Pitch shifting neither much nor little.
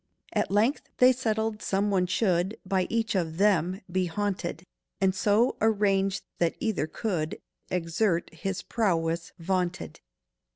Yes: average, 3.4 semitones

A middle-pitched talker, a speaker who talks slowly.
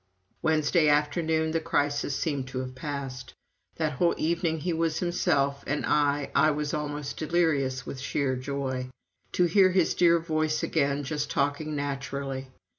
No: medium, 145 Hz; average, 150 wpm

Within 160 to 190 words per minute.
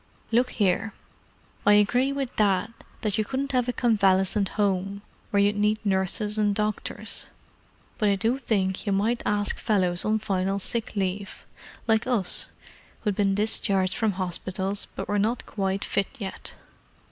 No: average, 145 wpm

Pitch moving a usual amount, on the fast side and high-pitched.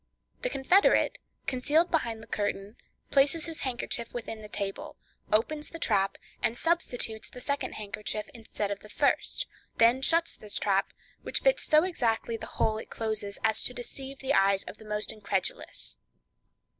No: average, 5.0 semitones; average, 160 wpm; high, 230 Hz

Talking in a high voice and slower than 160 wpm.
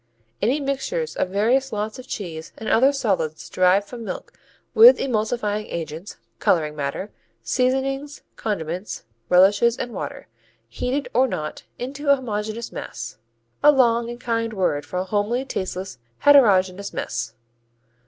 Yes: high, 215 Hz; average, 140 wpm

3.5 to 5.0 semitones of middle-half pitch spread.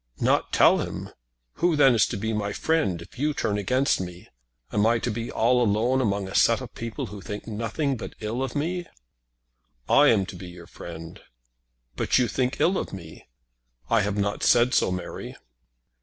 Yes: average, 4.6 semitones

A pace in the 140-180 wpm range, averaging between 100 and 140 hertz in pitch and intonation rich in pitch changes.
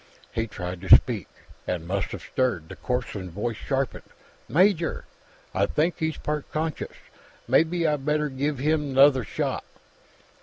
Yes: average, 145 wpm; low, 135 Hz; wide, 6.7 semitones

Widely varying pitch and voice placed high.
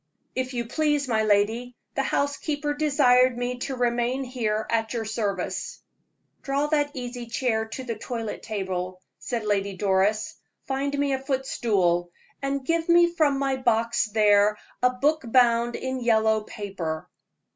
No: average, 4.0 semitones; high, 240 Hz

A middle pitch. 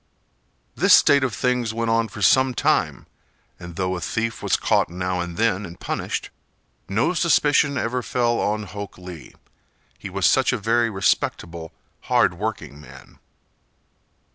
No: low, 105 Hz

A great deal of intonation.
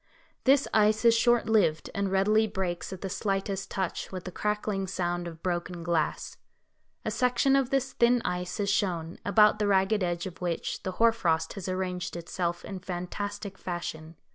No: average, 3.3 semitones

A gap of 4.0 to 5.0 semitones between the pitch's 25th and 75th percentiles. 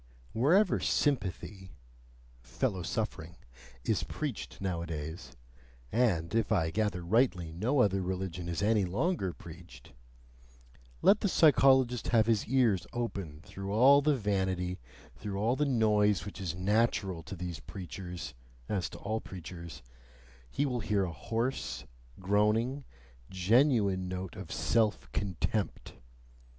Yes: average, 4.5 semitones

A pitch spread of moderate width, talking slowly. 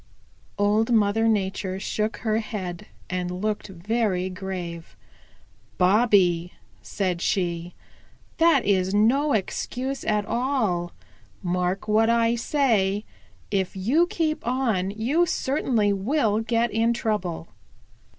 Yes: average, 4.0 semitones; slow, 110 wpm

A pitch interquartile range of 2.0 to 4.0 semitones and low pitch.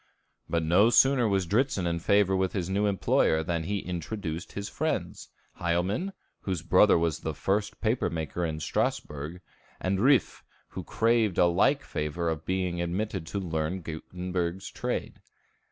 Yes: average, 3.4 semitones; very low, 90 Hz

